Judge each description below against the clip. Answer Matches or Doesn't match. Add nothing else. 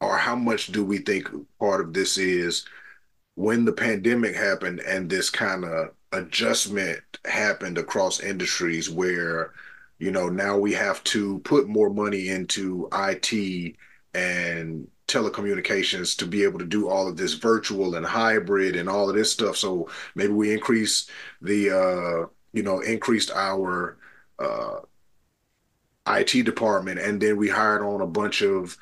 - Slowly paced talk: Doesn't match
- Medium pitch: Doesn't match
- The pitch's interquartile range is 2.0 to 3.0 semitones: Matches